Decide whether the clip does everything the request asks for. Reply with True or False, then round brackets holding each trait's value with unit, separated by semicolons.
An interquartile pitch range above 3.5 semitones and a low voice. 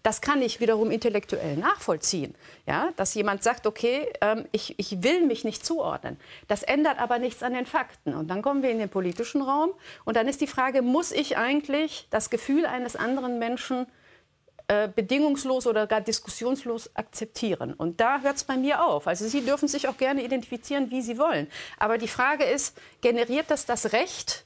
False (4.1 semitones; 245 Hz)